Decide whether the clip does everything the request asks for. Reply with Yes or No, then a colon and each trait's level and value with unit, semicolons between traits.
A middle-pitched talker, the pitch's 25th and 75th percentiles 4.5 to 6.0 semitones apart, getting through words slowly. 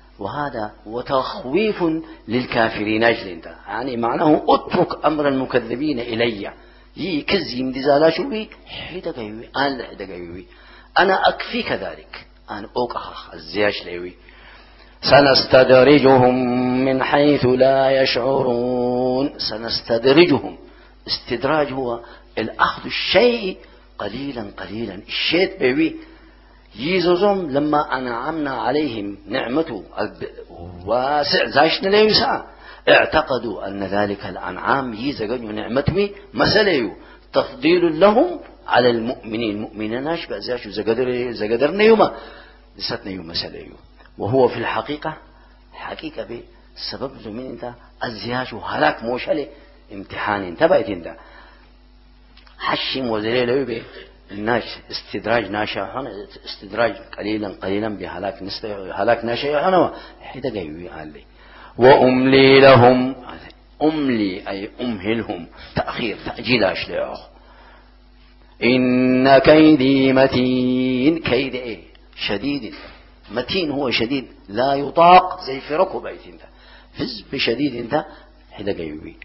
No: low, 125 Hz; average, 5.0 semitones; slow, 90 wpm